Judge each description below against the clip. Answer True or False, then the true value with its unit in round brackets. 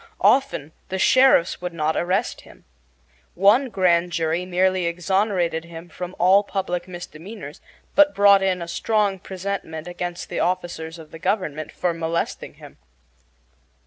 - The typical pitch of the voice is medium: True (180 Hz)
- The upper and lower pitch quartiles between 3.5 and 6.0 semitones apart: False (2.5 semitones)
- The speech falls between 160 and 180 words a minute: False (145 wpm)